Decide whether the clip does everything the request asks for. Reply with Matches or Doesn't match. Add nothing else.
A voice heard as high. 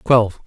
Doesn't match